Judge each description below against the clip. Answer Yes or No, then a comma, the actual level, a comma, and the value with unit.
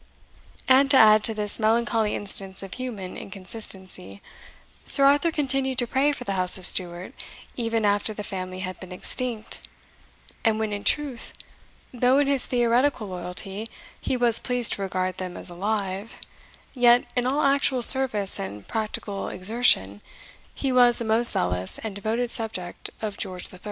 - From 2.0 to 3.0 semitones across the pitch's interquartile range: No, average, 4.6 semitones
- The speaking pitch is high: Yes, high, 220 Hz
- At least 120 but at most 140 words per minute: No, average, 160 wpm